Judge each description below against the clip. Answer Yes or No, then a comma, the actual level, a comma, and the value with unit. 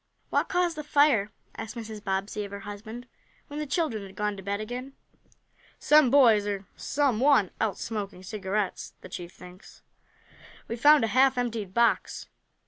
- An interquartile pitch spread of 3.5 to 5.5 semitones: Yes, average, 4.8 semitones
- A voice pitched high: Yes, high, 220 Hz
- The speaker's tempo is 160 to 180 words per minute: Yes, average, 165 wpm